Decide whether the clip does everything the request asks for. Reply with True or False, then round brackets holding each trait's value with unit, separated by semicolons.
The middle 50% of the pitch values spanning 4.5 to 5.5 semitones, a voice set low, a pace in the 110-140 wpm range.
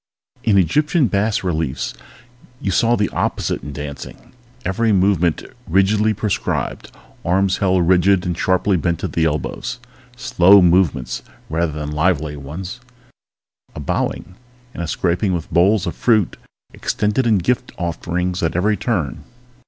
False (3.8 semitones; 90 Hz; 135 wpm)